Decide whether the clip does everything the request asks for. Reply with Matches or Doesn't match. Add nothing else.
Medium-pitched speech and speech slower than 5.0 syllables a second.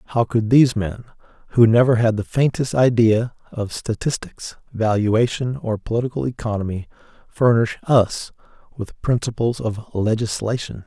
Doesn't match